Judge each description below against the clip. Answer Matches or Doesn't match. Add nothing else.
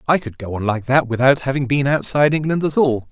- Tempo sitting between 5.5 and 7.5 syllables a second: Matches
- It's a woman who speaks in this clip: Doesn't match